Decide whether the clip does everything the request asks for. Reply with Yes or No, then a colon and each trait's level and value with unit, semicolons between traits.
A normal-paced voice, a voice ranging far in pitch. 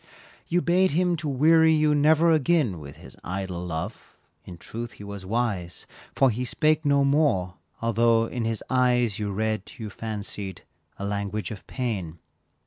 Yes: average, 160 wpm; wide, 6.7 semitones